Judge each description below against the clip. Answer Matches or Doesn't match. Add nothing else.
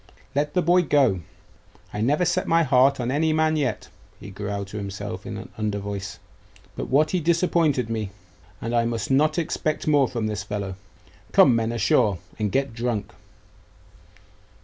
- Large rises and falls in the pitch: Matches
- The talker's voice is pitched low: Matches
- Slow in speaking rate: Doesn't match